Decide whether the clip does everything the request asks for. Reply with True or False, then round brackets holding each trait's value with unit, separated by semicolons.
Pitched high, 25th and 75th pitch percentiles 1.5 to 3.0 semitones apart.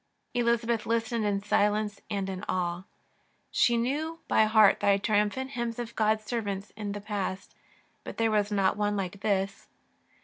True (210 Hz; 2.5 semitones)